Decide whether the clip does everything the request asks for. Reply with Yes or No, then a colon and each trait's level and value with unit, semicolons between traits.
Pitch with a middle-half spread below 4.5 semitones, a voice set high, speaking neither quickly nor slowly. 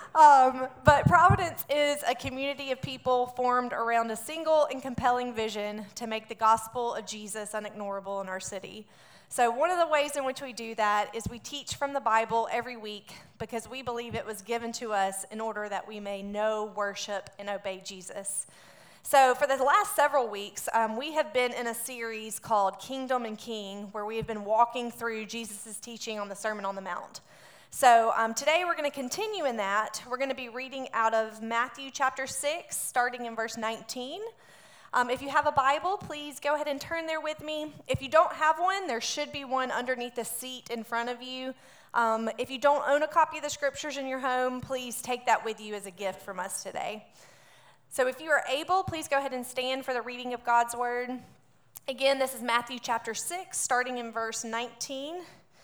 No: average, 3.6 semitones; high, 245 Hz; fast, 210 wpm